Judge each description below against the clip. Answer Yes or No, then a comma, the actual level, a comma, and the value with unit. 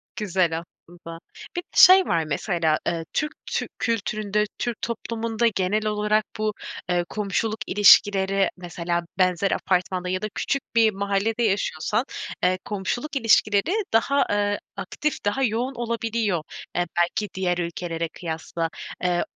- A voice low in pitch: No, high, 200 Hz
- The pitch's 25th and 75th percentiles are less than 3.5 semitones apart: No, average, 4.0 semitones